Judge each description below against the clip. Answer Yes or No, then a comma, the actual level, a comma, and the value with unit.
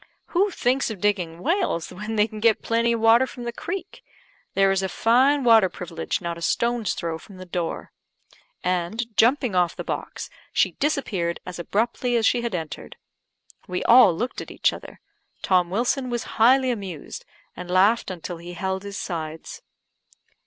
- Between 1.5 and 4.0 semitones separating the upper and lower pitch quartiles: No, average, 5.0 semitones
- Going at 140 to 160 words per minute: No, average, 175 wpm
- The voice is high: Yes, high, 210 Hz